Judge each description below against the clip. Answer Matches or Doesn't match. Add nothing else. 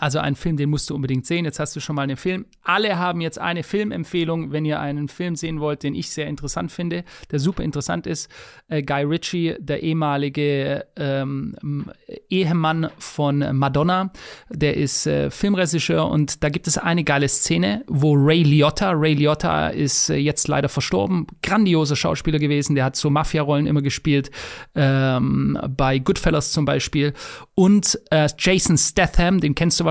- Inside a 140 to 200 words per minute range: Matches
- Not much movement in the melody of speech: Doesn't match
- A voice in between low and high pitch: Matches